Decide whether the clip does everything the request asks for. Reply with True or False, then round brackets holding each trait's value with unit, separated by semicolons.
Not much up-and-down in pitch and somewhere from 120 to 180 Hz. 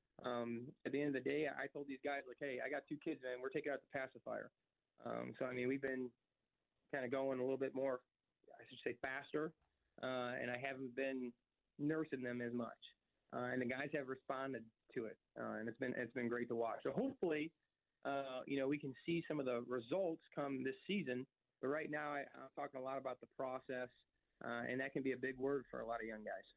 True (2.2 semitones; 130 Hz)